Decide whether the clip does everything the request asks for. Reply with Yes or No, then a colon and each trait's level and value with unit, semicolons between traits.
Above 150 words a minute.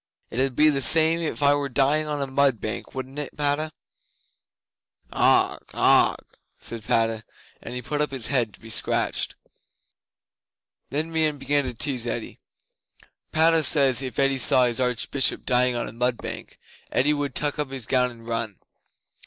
Yes: average, 170 wpm